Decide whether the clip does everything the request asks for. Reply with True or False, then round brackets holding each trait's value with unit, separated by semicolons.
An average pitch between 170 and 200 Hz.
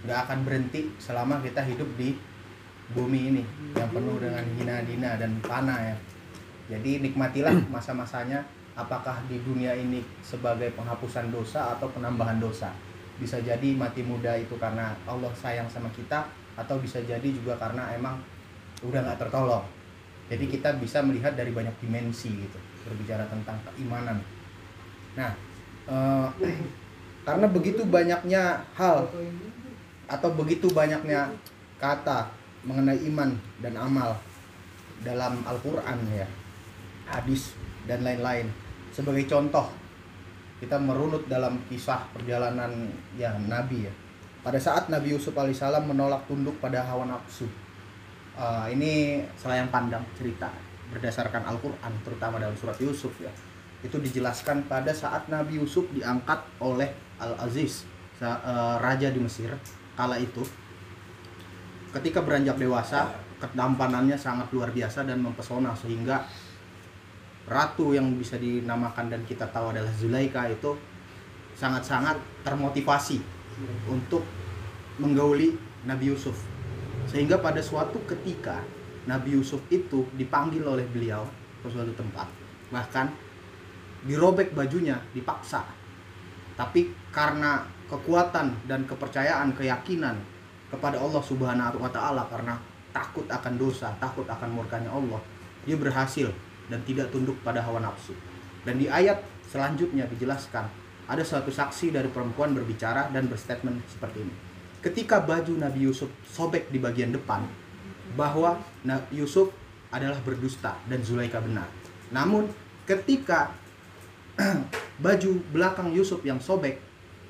False (125 Hz)